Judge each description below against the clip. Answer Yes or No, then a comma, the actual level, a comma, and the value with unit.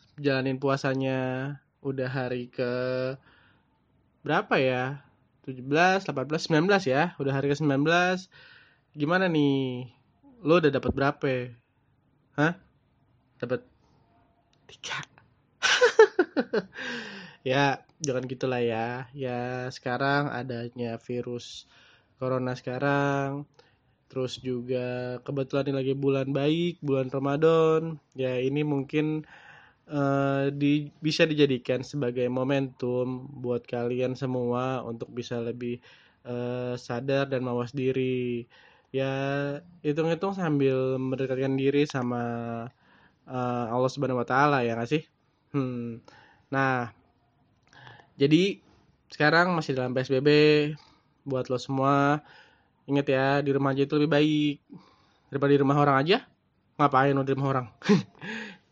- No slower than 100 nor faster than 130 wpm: Yes, average, 105 wpm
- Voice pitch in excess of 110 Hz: Yes, low, 135 Hz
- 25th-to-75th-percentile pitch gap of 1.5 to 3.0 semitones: Yes, narrow, 2.4 semitones